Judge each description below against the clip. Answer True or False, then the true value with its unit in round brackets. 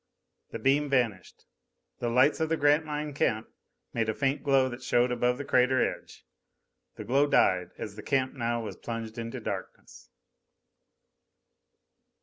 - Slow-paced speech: False (150 wpm)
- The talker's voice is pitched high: False (125 Hz)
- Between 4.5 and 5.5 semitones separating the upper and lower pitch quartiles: False (3.5 semitones)